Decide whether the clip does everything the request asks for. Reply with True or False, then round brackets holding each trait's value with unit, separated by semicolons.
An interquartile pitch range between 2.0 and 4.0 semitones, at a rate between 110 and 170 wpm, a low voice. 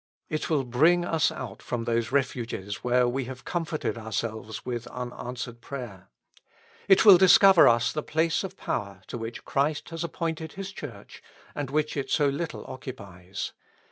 False (5.4 semitones; 165 wpm; 130 Hz)